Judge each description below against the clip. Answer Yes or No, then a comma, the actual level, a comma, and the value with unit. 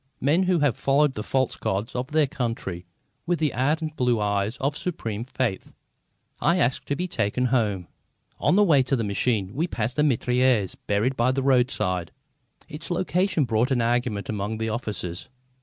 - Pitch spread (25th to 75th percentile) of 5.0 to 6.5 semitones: Yes, average, 5.3 semitones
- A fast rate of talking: No, average, 175 wpm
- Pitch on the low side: Yes, low, 125 Hz